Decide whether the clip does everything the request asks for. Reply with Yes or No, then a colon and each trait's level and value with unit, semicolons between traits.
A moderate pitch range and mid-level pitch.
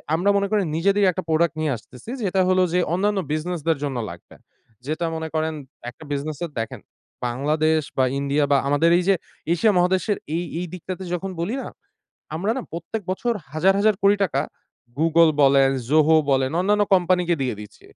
Yes: average, 3.8 semitones; medium, 170 Hz